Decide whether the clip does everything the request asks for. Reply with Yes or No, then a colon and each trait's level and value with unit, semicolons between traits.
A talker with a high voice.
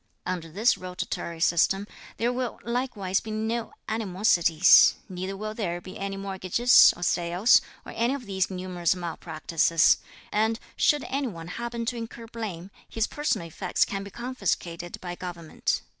Yes: high, 195 Hz